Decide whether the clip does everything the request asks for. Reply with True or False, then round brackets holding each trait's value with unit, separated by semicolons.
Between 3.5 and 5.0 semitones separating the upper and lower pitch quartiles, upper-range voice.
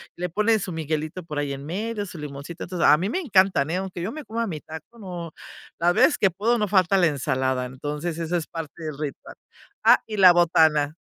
False (4.2 semitones; 170 Hz)